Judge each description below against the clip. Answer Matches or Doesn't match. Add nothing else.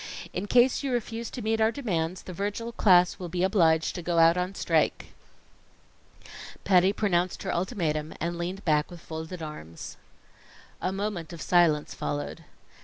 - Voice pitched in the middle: Matches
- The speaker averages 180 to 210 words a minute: Doesn't match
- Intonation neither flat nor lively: Matches